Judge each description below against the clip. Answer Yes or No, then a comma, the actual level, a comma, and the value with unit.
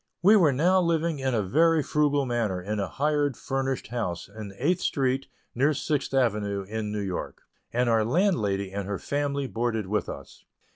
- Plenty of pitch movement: Yes, wide, 5.9 semitones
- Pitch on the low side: Yes, low, 125 Hz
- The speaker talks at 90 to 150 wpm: No, average, 180 wpm